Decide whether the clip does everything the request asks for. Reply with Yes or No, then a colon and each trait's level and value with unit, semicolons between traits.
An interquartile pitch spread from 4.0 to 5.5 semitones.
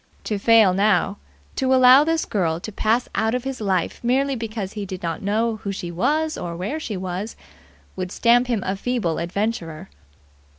Yes: average, 4.8 semitones